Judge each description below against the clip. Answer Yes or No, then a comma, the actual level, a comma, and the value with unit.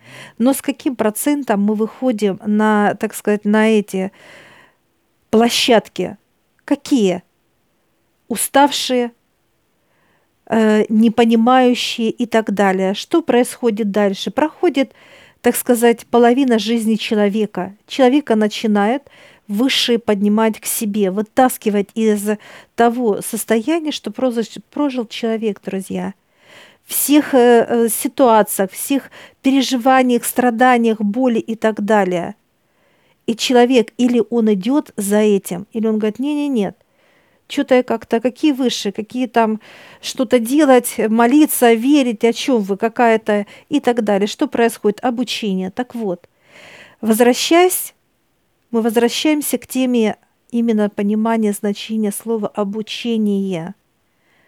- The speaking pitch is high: Yes, high, 230 Hz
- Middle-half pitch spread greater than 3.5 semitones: No, average, 3.1 semitones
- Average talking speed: No, slow, 105 wpm